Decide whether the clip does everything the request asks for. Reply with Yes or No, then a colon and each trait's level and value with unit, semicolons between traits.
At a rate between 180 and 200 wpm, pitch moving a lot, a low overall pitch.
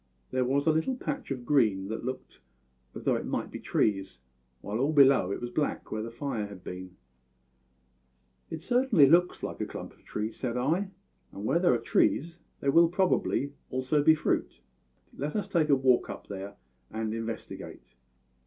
Yes: average, 185 wpm; wide, 6.3 semitones; low, 130 Hz